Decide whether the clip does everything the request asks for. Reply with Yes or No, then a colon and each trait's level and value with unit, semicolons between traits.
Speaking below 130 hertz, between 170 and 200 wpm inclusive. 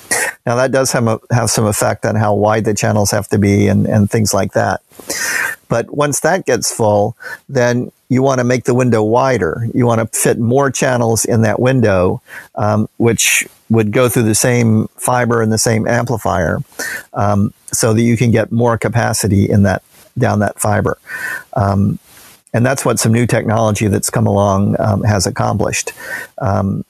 Yes: low, 115 Hz; average, 185 wpm